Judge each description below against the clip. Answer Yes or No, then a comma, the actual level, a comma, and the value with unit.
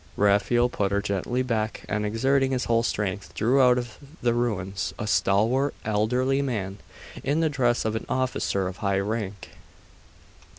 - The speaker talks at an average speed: Yes, average, 160 wpm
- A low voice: Yes, low, 115 Hz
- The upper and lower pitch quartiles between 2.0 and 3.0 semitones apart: No, average, 3.8 semitones